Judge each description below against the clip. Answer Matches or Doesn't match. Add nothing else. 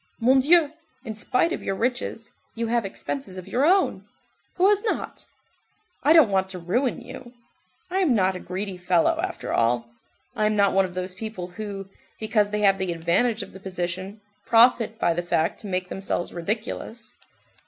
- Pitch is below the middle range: Doesn't match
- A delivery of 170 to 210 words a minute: Matches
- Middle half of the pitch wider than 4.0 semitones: Matches